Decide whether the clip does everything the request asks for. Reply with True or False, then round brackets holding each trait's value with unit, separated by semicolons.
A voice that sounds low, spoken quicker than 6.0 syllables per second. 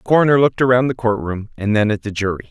True (115 Hz; 7.3 syllables/s)